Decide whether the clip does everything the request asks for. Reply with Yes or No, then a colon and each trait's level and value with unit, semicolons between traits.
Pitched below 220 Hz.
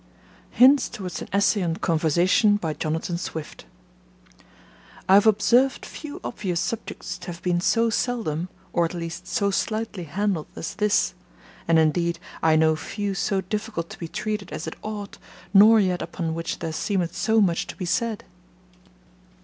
Yes: high, 190 Hz